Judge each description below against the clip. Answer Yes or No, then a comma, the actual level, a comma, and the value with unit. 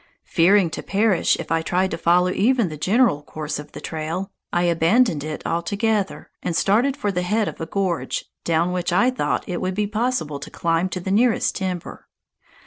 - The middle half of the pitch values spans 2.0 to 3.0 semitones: No, average, 3.9 semitones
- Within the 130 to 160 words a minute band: No, average, 195 wpm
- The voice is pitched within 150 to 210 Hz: Yes, medium, 185 Hz